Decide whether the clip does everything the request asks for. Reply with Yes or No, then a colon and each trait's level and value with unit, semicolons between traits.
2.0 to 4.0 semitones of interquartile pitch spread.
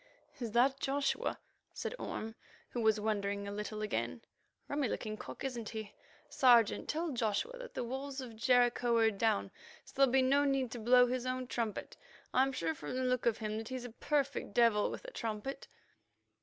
Yes: average, 3.4 semitones